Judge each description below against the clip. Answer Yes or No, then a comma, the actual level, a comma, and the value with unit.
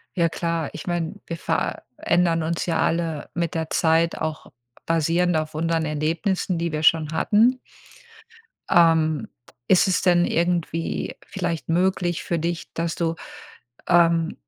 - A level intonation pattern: Yes, narrow, 1.3 semitones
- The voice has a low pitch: No, medium, 165 Hz